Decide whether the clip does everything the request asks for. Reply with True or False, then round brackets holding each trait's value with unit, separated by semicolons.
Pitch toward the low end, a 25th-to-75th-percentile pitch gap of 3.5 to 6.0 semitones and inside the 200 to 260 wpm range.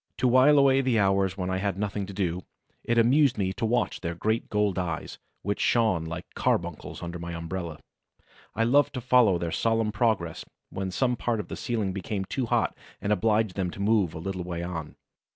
True (100 Hz; 4.2 semitones; 205 wpm)